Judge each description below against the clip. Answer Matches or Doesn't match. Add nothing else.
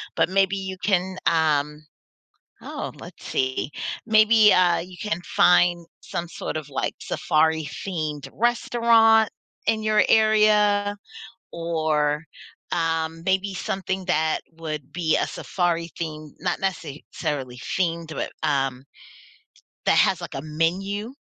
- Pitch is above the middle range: Doesn't match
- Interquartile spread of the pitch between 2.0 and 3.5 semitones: Doesn't match